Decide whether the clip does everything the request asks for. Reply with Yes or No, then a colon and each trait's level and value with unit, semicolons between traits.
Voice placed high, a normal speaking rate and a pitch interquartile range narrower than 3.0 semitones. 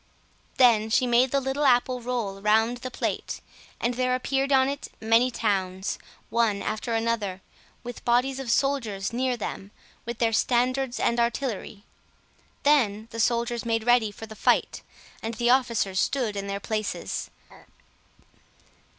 Yes: high, 235 Hz; average, 150 wpm; narrow, 2.6 semitones